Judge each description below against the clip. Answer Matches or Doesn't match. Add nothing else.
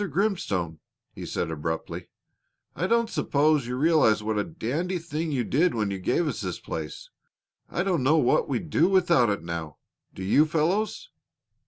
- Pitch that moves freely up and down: Matches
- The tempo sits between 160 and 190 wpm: Matches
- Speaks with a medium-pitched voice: Matches